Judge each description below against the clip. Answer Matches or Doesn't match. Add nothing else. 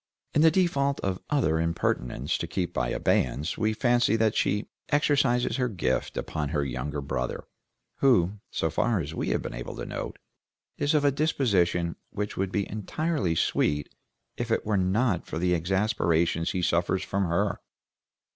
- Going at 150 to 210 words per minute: Matches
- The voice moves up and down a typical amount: Doesn't match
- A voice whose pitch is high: Doesn't match